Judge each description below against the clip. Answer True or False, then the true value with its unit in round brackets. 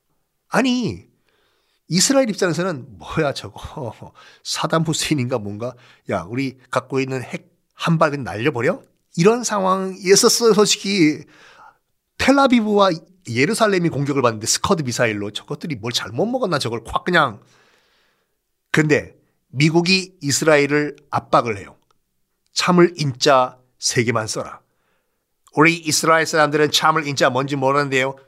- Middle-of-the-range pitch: True (155 Hz)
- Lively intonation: True (6.0 semitones)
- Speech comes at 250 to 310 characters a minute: True (280 characters per minute)